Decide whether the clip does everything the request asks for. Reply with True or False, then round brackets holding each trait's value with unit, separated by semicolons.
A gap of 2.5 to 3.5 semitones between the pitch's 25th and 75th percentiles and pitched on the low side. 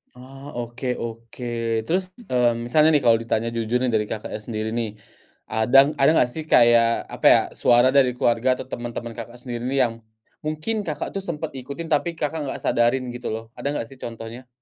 True (3.1 semitones; 120 Hz)